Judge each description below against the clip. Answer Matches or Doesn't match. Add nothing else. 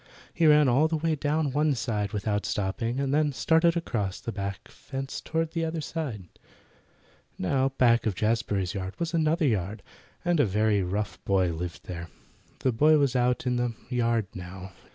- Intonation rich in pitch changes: Matches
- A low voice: Matches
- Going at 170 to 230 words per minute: Matches